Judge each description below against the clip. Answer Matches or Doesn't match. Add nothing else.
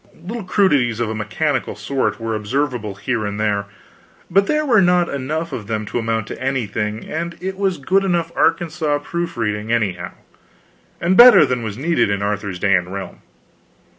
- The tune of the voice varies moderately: Doesn't match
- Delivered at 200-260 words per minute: Doesn't match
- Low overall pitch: Matches